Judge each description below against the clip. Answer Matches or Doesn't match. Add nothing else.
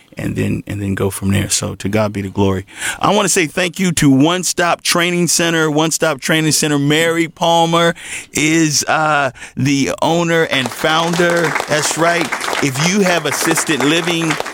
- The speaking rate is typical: Matches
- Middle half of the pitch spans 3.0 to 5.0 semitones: Matches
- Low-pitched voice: Doesn't match